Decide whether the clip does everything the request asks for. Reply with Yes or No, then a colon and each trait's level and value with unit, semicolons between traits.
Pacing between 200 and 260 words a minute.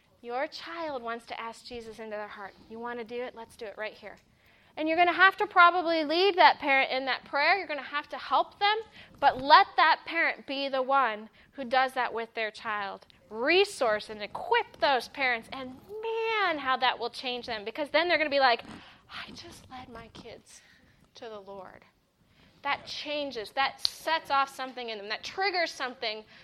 Yes: fast, 205 wpm